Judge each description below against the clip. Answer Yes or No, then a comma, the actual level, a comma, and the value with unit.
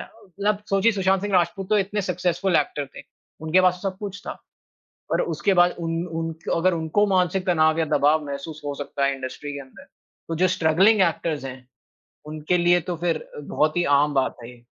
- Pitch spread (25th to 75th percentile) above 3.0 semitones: Yes, average, 3.5 semitones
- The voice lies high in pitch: No, medium, 170 Hz